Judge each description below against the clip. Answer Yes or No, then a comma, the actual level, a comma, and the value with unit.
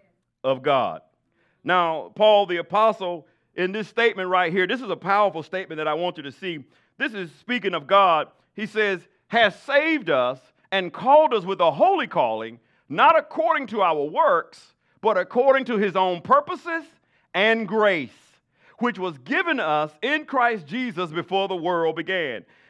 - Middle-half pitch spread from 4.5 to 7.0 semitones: Yes, wide, 5.6 semitones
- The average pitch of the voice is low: No, high, 195 Hz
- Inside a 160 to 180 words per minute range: Yes, average, 165 wpm